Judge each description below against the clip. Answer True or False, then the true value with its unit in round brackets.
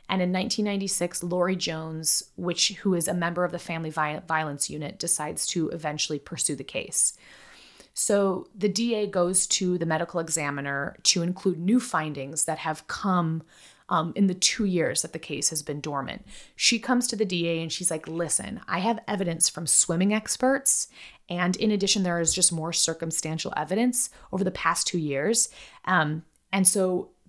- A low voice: False (175 Hz)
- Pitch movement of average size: True (3.2 semitones)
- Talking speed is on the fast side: False (175 wpm)